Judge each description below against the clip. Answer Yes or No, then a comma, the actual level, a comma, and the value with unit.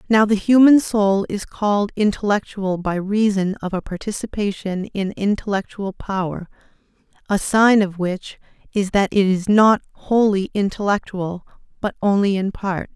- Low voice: No, high, 200 Hz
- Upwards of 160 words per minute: No, average, 140 wpm